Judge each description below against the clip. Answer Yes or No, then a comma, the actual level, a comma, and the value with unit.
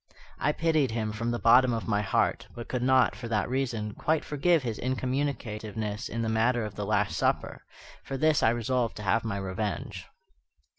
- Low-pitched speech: Yes, low, 115 Hz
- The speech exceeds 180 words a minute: Yes, average, 190 wpm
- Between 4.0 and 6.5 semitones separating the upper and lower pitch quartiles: No, average, 3.4 semitones